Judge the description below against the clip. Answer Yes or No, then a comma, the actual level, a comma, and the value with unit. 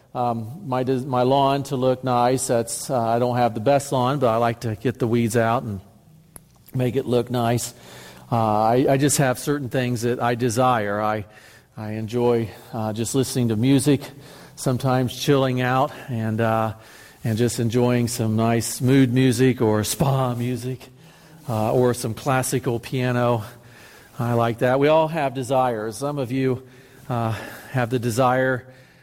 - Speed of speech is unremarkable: Yes, average, 165 wpm